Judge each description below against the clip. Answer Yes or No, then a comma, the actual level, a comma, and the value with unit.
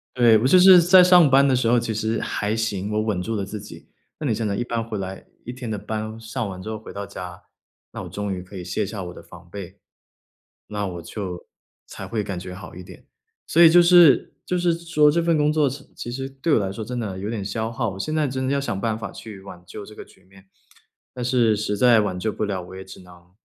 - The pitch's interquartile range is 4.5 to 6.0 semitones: Yes, average, 5.1 semitones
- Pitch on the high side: No, low, 110 Hz